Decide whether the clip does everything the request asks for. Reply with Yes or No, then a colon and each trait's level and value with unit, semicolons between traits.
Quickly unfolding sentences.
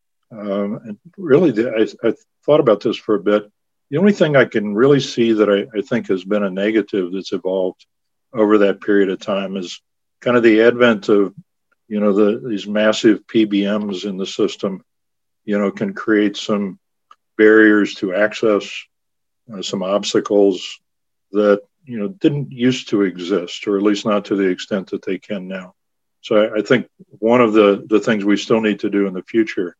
No: average, 195 wpm